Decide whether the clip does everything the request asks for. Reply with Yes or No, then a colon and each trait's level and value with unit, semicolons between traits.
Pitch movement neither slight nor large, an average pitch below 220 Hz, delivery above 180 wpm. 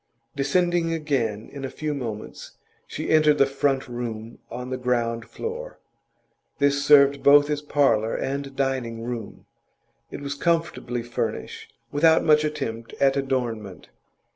No: average, 3.7 semitones; low, 135 Hz; slow, 135 wpm